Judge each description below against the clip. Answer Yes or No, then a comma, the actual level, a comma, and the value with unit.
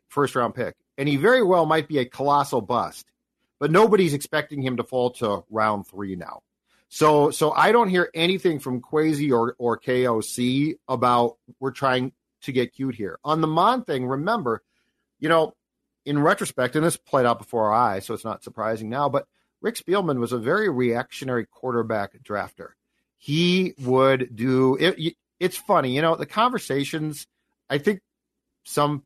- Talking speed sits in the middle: Yes, average, 170 wpm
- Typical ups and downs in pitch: Yes, average, 4.5 semitones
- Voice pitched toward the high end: No, medium, 140 Hz